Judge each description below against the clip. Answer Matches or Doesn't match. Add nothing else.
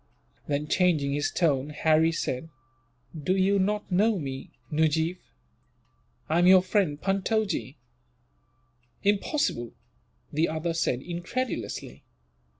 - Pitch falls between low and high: Matches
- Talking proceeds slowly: Matches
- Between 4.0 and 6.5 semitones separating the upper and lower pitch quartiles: Matches